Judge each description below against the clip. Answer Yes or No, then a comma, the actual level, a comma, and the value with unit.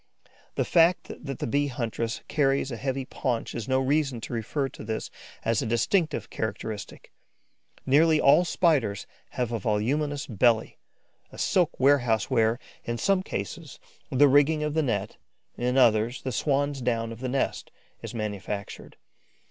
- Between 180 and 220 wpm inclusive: No, average, 155 wpm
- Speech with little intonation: No, average, 4.0 semitones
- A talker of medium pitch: No, low, 130 Hz